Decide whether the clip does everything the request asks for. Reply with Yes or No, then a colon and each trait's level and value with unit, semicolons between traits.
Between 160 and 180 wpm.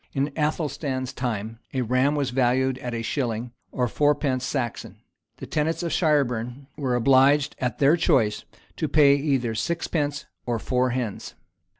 No: average, 150 wpm